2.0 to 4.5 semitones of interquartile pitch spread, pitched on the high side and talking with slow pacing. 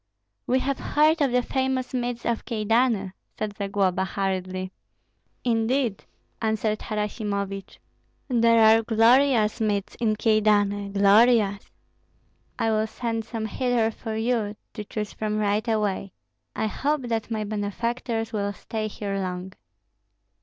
Yes: narrow, 2.5 semitones; high, 220 Hz; slow, 125 wpm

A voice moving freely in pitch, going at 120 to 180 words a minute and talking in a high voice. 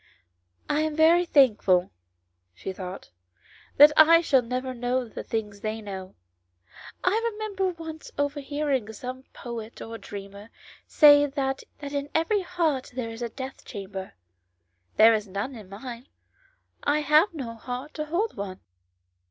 Yes: wide, 5.8 semitones; average, 150 wpm; very high, 260 Hz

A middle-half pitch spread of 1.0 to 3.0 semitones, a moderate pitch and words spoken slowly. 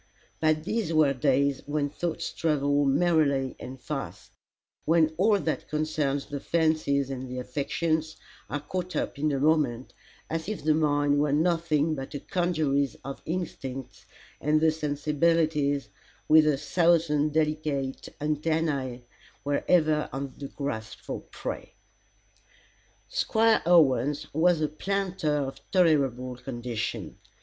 Yes: narrow, 2.5 semitones; medium, 150 Hz; slow, 130 wpm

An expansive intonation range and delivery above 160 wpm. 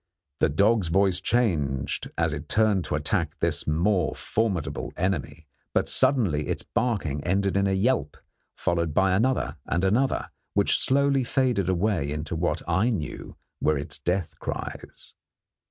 No: wide, 5.7 semitones; average, 145 wpm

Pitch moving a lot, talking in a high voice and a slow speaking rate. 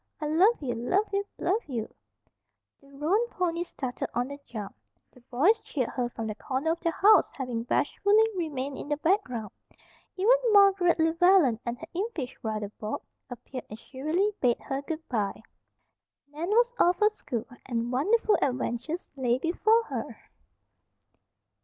No: wide, 7.5 semitones; very high, 300 Hz; average, 155 wpm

